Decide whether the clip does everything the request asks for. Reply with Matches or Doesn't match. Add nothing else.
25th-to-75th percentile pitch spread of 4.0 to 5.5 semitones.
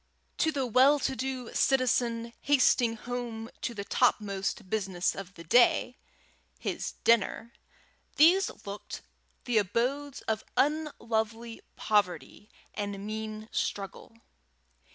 Doesn't match